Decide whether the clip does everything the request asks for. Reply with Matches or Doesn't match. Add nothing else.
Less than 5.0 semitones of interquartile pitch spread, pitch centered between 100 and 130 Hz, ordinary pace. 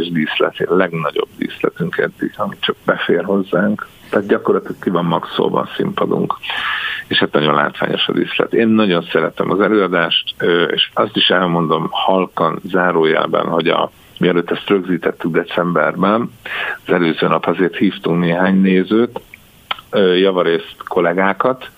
Doesn't match